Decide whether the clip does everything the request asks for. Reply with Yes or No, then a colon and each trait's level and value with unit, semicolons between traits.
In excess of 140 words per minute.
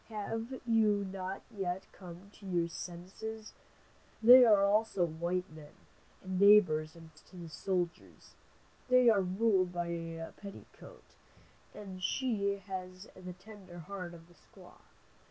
No: slow, 135 wpm